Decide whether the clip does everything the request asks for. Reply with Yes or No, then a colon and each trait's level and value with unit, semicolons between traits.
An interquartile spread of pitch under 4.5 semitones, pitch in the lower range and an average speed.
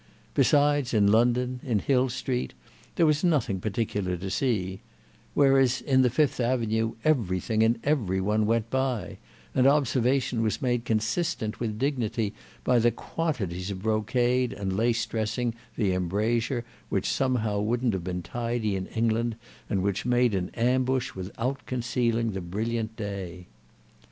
Yes: average, 3.6 semitones; low, 115 Hz; average, 145 wpm